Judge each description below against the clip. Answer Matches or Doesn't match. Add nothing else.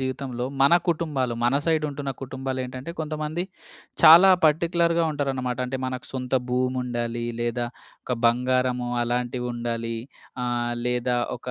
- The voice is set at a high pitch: Doesn't match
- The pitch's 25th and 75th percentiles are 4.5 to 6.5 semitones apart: Doesn't match